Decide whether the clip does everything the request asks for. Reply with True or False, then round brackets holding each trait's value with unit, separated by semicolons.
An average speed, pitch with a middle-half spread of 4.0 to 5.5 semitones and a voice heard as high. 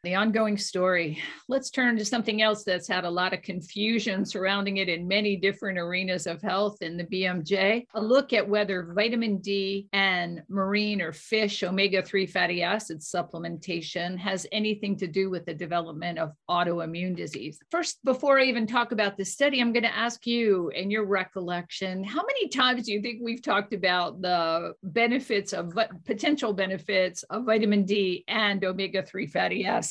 False (175 wpm; 3.2 semitones; 195 Hz)